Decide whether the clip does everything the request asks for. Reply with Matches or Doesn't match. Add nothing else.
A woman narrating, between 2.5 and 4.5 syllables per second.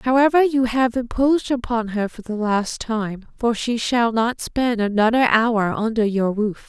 Matches